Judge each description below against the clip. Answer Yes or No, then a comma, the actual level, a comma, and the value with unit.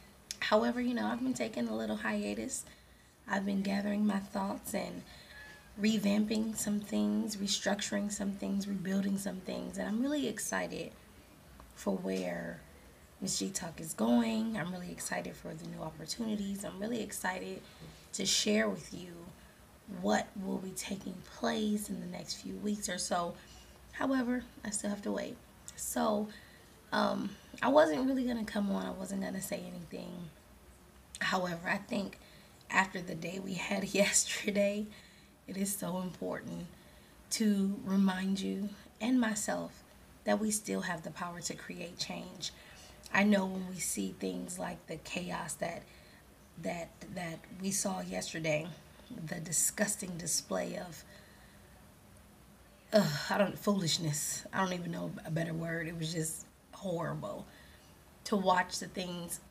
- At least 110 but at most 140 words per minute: No, average, 150 wpm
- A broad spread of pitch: No, average, 4.0 semitones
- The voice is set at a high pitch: Yes, high, 195 Hz